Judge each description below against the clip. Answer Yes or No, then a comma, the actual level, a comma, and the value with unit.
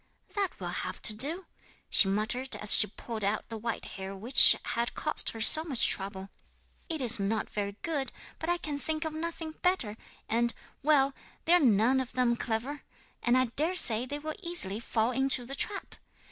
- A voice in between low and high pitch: No, very high, 250 Hz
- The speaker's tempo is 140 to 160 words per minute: No, average, 190 wpm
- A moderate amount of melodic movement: No, wide, 6.1 semitones